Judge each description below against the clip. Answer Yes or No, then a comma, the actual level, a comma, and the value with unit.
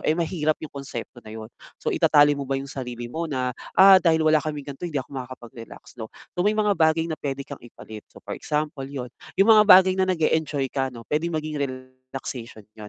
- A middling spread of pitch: Yes, average, 3.8 semitones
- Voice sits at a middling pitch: Yes, medium, 145 Hz